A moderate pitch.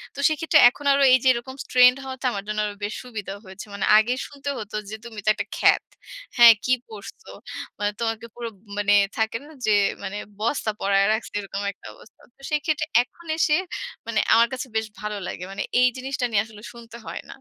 No: high, 225 Hz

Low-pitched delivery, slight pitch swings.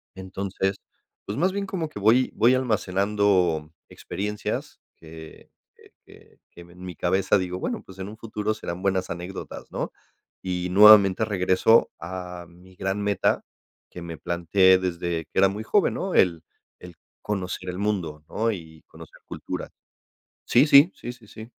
No: very low, 95 Hz; average, 3.0 semitones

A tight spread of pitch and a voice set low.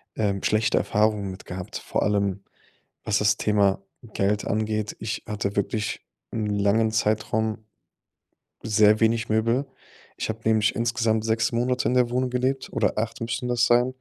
Yes: narrow, 1.8 semitones; low, 110 Hz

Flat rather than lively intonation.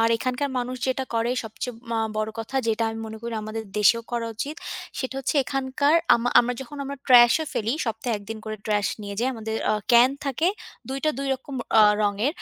No: average, 3.0 semitones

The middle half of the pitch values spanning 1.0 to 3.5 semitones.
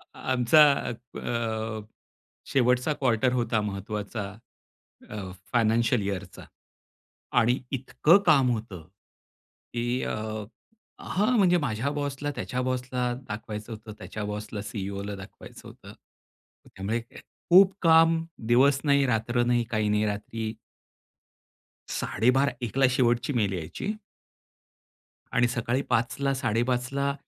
No: average, 4.0 semitones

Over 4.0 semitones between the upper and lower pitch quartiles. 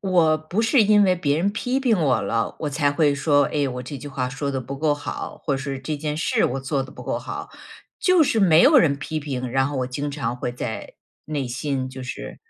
No: average, 3.4 semitones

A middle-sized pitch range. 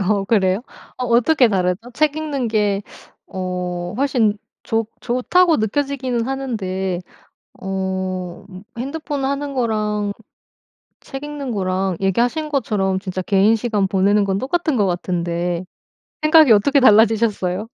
No: wide, 5.9 semitones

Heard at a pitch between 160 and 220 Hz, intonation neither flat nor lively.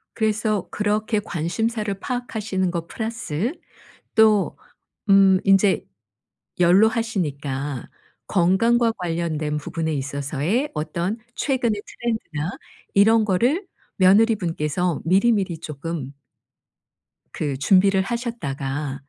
No: high, 190 Hz; wide, 5.8 semitones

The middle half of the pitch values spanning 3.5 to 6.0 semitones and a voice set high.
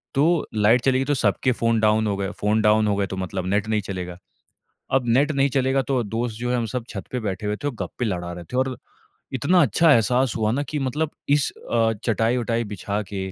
No: average, 4.0 semitones; low, 115 Hz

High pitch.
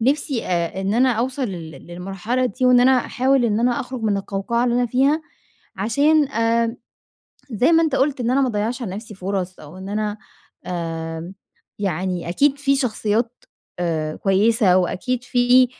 Yes: high, 230 Hz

